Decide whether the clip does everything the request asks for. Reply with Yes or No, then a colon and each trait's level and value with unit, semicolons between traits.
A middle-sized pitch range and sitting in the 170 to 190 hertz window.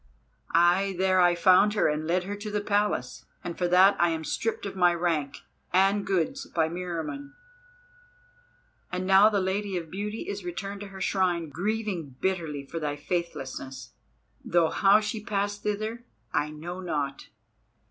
Yes: average, 3.5 semitones; medium, 185 Hz